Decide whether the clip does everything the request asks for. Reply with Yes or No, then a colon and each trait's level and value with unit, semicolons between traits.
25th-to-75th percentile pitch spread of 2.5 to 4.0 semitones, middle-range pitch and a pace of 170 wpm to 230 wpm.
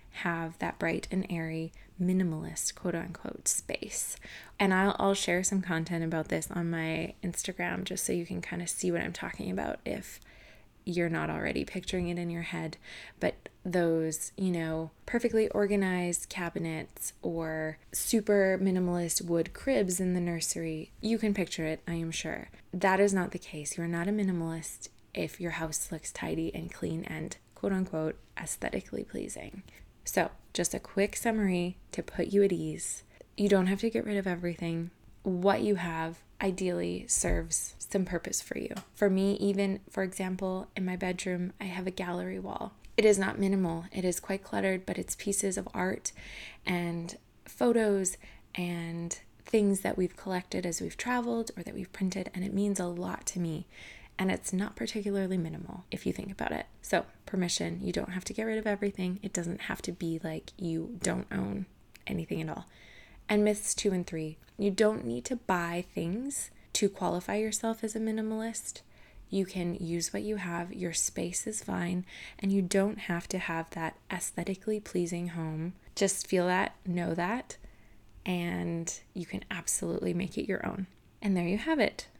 Yes: average, 3.0 semitones; medium, 180 Hz; average, 180 wpm